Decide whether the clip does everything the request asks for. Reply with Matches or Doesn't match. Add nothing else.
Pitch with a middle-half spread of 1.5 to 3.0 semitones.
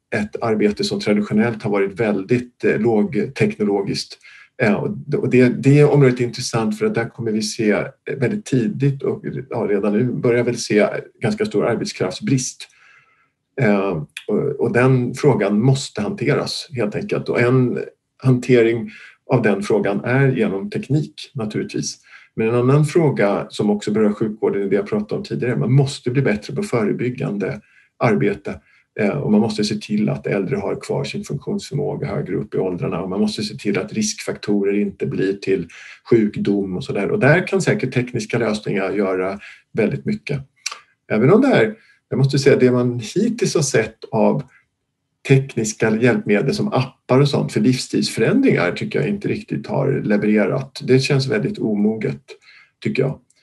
Doesn't match